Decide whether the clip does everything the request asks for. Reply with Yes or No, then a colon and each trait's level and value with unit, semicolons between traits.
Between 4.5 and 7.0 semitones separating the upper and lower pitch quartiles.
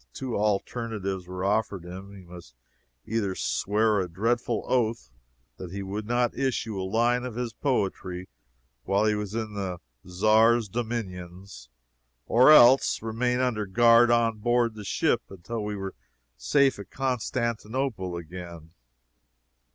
No: average, 4.0 semitones